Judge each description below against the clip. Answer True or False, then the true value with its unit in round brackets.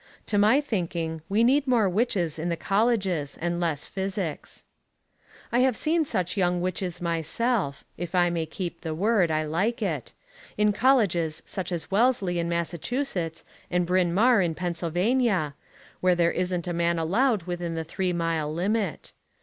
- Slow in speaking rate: False (160 wpm)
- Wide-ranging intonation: False (3.9 semitones)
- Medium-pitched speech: True (180 Hz)